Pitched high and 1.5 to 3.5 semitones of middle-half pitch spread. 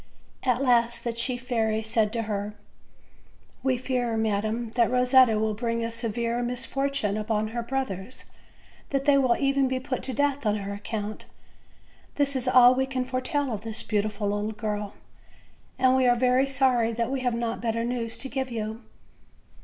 Yes: high, 235 Hz; average, 2.9 semitones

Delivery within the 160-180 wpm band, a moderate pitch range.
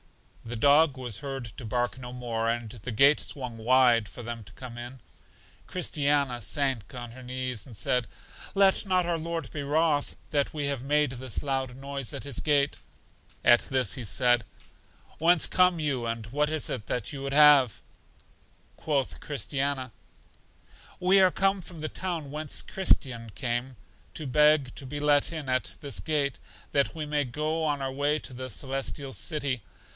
Yes: average, 175 wpm; average, 3.3 semitones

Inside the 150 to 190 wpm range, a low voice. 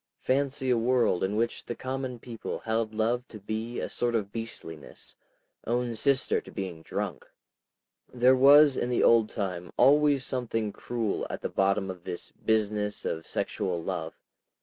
Yes: average, 160 wpm; low, 115 Hz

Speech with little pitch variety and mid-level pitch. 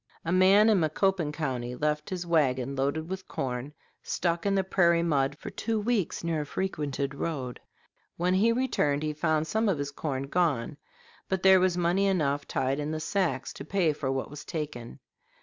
No: average, 4.8 semitones; medium, 155 Hz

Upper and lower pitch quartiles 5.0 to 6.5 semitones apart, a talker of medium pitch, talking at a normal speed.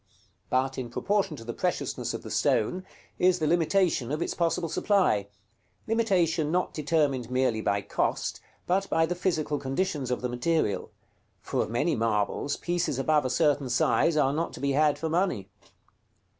Yes: wide, 5.4 semitones; medium, 150 Hz; average, 170 wpm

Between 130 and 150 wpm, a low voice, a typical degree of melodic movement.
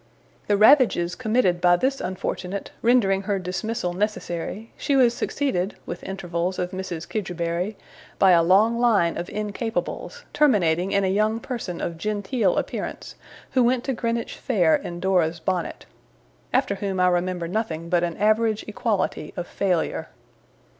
No: average, 145 wpm; high, 195 Hz; average, 4.2 semitones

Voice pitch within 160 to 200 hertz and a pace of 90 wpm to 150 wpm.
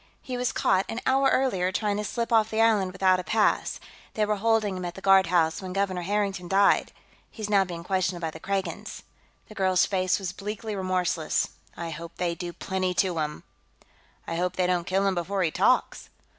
No: high, 190 Hz; average, 200 wpm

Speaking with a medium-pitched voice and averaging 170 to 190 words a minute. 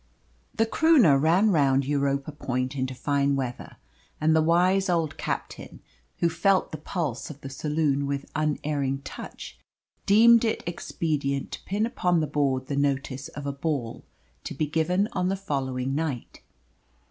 No: medium, 150 Hz; average, 155 wpm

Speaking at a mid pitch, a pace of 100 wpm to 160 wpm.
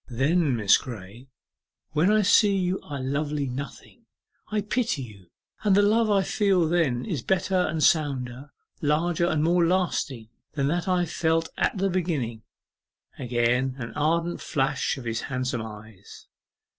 Yes: medium, 150 Hz; average, 155 wpm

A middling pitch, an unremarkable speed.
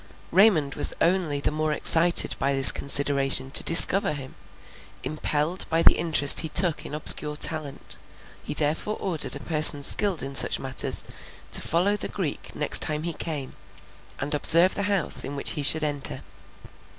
Yes: medium, 155 Hz; average, 170 wpm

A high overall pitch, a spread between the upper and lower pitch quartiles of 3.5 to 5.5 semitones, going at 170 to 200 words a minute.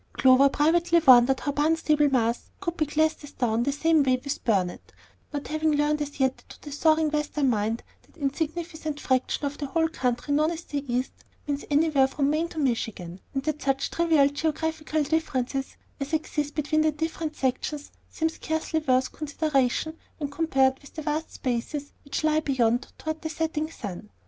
No: very high, 295 Hz; average, 2.9 semitones; average, 180 wpm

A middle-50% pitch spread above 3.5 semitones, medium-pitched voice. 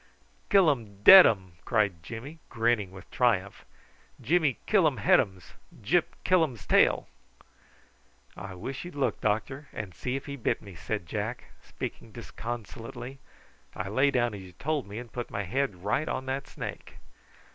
No: wide, 5.4 semitones; low, 115 Hz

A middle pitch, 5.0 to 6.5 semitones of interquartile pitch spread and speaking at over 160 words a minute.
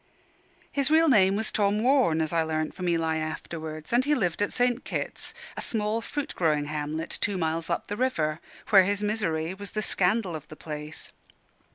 Yes: medium, 180 Hz; wide, 5.4 semitones; average, 190 wpm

